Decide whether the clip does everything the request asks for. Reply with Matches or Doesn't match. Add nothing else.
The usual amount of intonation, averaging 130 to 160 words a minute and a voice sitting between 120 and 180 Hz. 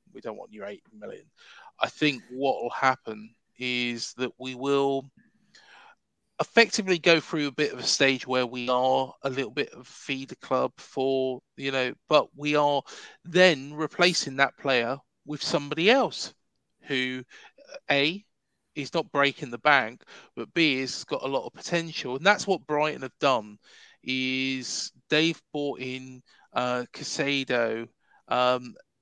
Matches